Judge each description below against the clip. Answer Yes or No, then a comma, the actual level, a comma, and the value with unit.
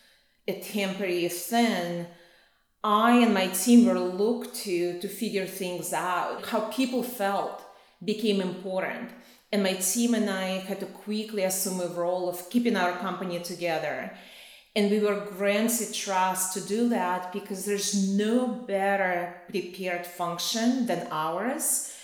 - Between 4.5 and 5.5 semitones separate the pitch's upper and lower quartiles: No, average, 3.2 semitones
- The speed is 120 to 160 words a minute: Yes, average, 140 wpm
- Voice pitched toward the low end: No, high, 195 Hz